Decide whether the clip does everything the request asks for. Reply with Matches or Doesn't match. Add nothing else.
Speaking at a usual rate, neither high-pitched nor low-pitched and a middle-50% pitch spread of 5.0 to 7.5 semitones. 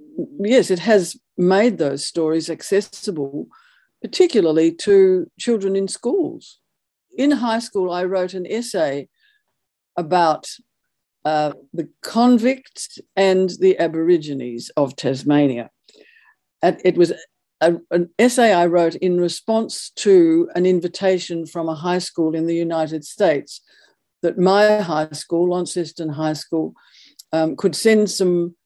Doesn't match